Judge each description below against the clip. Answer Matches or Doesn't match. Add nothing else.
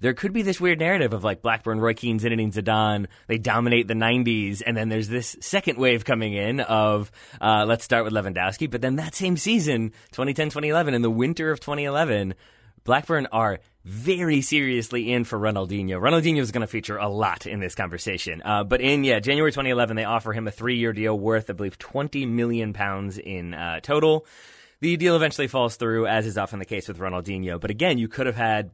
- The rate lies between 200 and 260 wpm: Matches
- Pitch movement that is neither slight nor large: Matches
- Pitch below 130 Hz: Matches